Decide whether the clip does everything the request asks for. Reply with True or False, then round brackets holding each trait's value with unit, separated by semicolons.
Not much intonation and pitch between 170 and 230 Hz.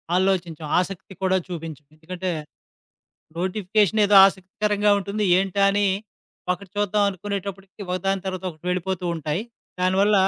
True (1.9 semitones; 190 Hz)